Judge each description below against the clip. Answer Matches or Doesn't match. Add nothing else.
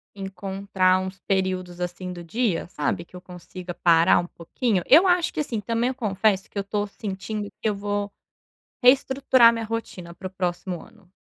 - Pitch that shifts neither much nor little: Matches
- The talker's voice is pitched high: Matches